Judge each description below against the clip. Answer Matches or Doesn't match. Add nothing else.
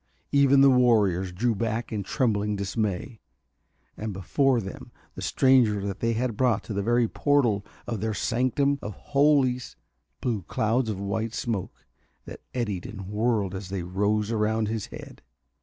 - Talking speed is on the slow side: Doesn't match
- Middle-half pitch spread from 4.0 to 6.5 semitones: Doesn't match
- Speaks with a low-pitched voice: Matches